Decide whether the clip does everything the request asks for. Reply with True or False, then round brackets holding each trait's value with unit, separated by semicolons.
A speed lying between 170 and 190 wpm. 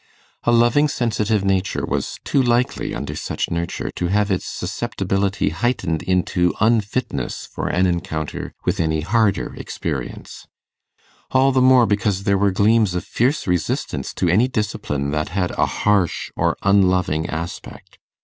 False (145 wpm)